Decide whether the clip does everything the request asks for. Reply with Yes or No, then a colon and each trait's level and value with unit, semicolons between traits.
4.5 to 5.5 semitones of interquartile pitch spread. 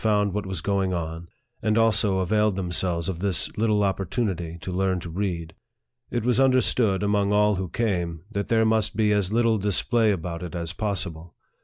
No: average, 3.5 semitones